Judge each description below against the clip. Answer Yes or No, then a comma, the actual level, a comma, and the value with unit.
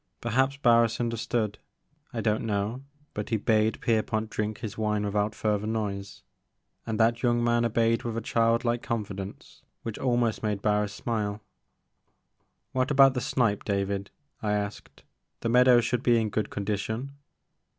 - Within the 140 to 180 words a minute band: Yes, average, 155 wpm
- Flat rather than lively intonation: Yes, narrow, 2.2 semitones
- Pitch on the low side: Yes, low, 110 Hz